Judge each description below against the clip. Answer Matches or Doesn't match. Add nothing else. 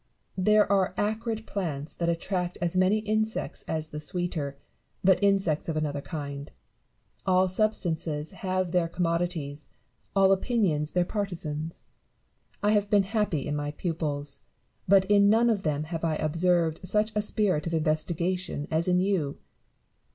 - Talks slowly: Doesn't match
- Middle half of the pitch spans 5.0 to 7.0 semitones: Doesn't match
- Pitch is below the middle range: Doesn't match